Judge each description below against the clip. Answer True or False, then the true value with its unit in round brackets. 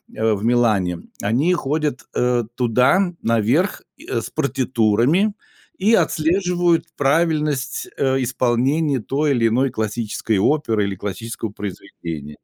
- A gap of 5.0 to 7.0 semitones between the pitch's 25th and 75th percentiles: True (5.6 semitones)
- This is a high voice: False (125 Hz)